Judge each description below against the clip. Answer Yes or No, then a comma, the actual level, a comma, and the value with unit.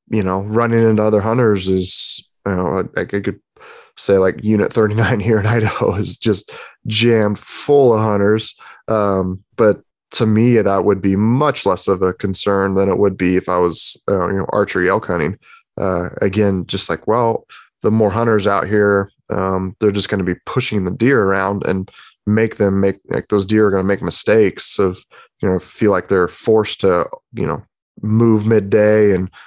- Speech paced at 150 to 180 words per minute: No, average, 195 wpm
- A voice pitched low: Yes, low, 100 Hz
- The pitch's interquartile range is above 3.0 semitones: No, narrow, 2.4 semitones